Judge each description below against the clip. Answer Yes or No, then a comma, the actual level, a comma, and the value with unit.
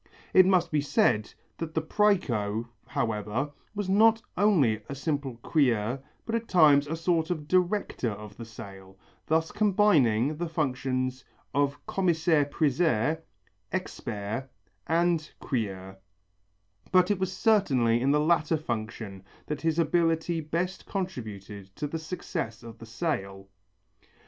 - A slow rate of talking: Yes, slow, 130 wpm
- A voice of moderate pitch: Yes, medium, 150 Hz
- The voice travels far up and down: Yes, wide, 7.0 semitones